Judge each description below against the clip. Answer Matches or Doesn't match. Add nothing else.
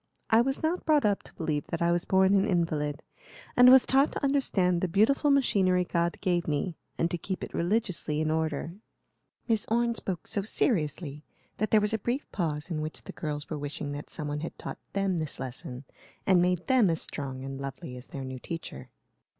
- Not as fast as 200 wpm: Doesn't match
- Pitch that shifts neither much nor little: Doesn't match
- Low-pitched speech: Doesn't match